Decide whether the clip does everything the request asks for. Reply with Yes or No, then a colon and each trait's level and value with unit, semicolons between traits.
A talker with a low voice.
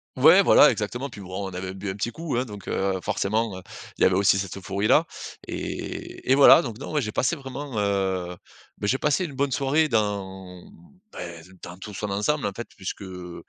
Yes: low, 105 Hz